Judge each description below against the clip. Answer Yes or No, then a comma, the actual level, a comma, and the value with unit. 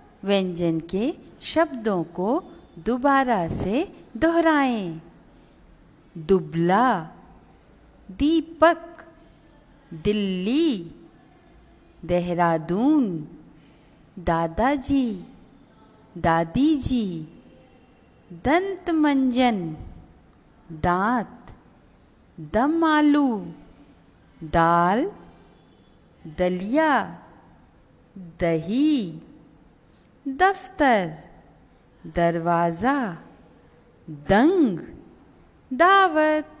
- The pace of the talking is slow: Yes, slow, 40 wpm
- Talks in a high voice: Yes, high, 200 Hz